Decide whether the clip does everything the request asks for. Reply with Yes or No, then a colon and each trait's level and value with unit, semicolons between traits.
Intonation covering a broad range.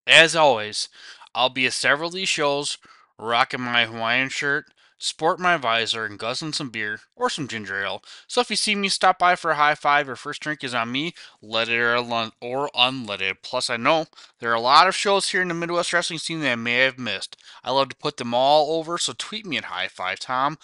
Yes: wide, 5.8 semitones